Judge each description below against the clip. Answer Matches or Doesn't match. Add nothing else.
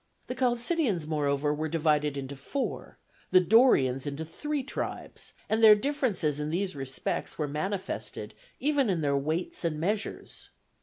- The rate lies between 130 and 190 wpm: Matches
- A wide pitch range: Matches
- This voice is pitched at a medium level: Matches